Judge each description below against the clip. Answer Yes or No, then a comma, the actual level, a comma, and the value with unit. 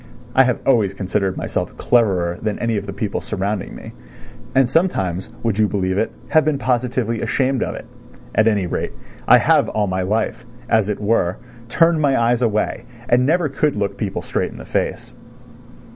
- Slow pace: No, average, 185 wpm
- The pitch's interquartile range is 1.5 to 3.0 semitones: No, average, 4.3 semitones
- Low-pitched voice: Yes, low, 110 Hz